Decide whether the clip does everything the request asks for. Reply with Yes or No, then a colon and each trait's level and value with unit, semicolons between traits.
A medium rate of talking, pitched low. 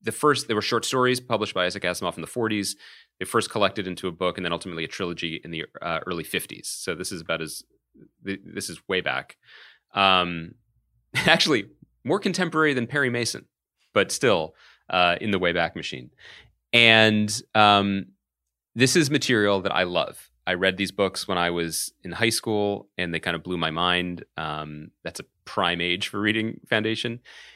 Yes: average, 185 wpm; low, 100 Hz